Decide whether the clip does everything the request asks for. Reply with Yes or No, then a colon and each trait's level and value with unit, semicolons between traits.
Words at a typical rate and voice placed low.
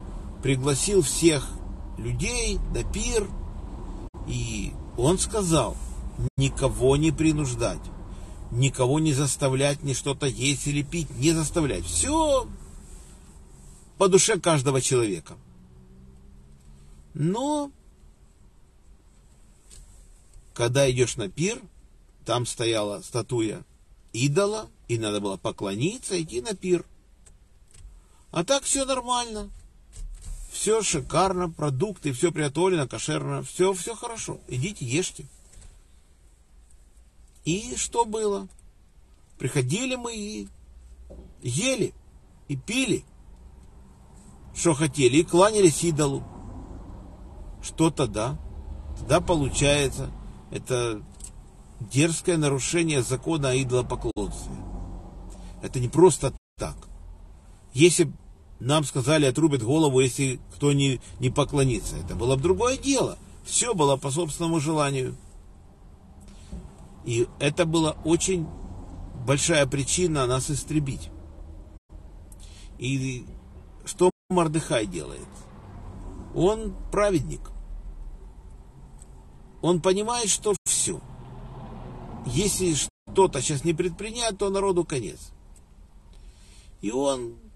No: slow, 90 wpm; low, 130 Hz